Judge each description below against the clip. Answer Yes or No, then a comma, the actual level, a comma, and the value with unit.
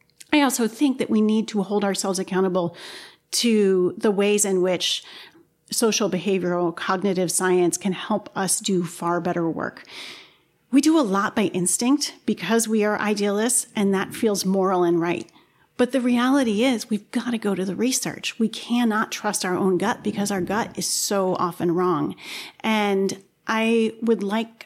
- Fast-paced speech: No, average, 170 wpm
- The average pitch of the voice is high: Yes, high, 205 Hz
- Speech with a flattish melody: No, average, 3.7 semitones